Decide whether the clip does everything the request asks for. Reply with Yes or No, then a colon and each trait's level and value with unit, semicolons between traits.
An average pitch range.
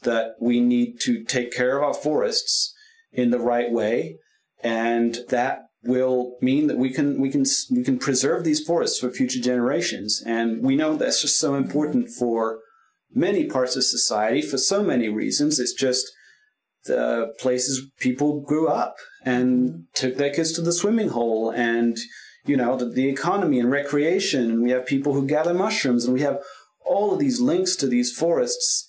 Yes: average, 3.7 semitones